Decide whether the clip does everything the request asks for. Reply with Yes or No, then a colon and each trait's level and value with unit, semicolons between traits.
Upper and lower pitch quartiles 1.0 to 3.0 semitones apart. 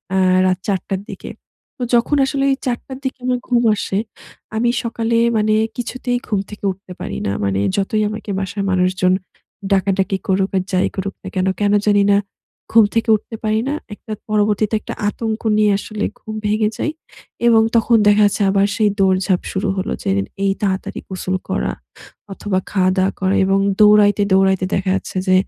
Yes: narrow, 2.5 semitones